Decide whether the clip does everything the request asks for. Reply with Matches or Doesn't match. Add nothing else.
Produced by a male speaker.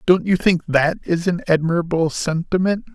Matches